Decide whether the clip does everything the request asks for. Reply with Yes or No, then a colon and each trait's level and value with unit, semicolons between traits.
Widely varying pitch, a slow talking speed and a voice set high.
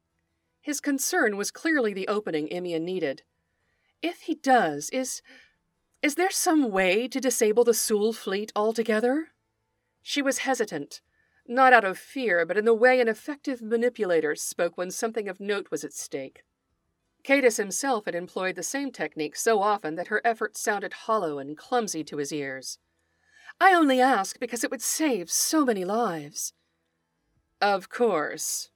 No: wide, 6.5 semitones; average, 155 wpm; high, 225 Hz